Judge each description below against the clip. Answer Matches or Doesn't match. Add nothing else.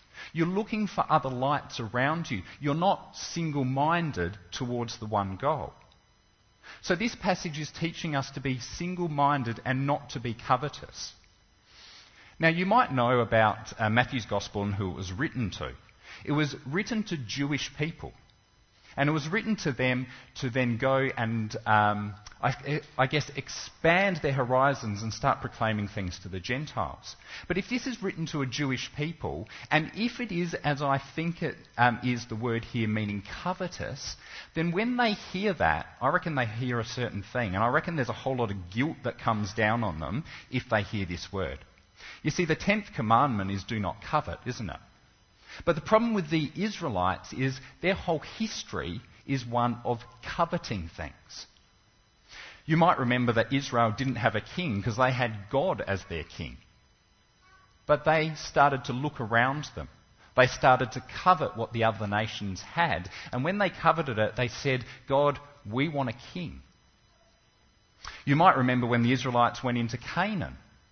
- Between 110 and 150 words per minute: Doesn't match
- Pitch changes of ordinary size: Doesn't match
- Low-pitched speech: Matches